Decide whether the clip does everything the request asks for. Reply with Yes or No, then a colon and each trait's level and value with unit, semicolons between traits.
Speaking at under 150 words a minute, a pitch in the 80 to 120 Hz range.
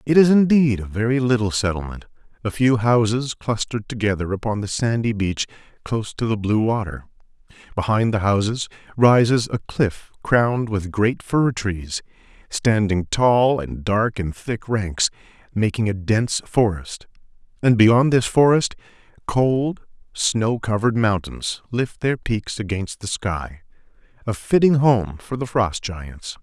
Yes: average, 140 wpm; low, 110 Hz